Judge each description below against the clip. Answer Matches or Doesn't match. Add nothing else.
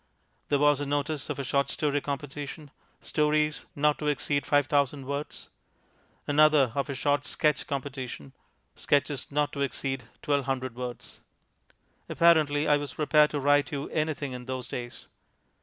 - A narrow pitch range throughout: Matches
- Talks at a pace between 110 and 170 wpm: Matches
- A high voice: Doesn't match